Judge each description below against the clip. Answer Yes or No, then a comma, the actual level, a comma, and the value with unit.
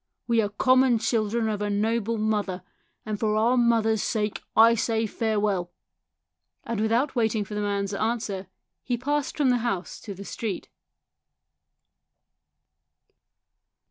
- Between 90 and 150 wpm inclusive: Yes, slow, 135 wpm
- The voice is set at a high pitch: Yes, high, 220 Hz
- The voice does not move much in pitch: Yes, narrow, 2.2 semitones